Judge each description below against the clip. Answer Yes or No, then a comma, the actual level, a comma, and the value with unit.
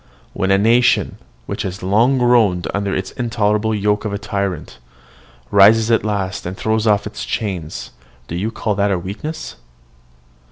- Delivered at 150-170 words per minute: Yes, average, 155 wpm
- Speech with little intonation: Yes, narrow, 2.3 semitones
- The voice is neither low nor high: No, low, 105 Hz